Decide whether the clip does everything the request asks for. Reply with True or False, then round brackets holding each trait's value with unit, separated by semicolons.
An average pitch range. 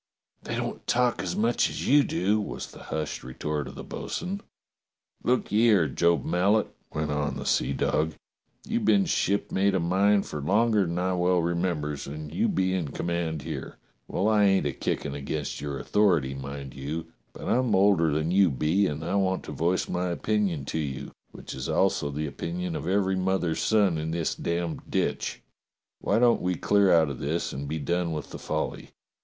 True (4.6 semitones)